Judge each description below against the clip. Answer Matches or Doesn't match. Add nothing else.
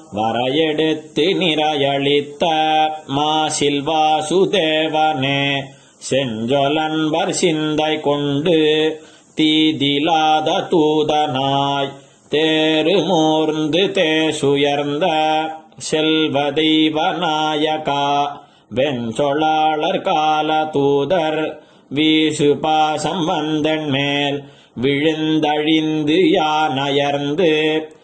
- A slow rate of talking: Matches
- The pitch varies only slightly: Matches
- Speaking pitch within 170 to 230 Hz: Doesn't match